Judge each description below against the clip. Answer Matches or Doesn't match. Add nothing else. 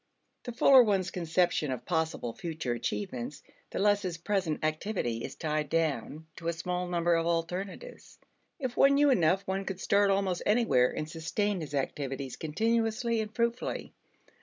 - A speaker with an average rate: Matches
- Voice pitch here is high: Doesn't match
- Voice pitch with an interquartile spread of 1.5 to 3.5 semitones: Doesn't match